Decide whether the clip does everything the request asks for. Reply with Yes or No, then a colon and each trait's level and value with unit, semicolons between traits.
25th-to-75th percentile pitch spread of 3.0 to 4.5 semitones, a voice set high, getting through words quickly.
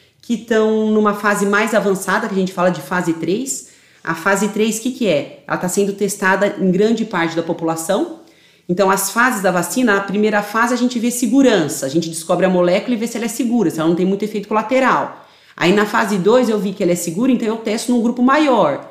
Yes: average, 4.0 semitones; high, 205 Hz; fast, 240 wpm